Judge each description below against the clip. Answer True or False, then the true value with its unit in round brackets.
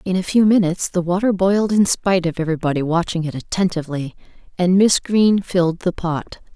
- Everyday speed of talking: True (185 wpm)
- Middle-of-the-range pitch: True (180 Hz)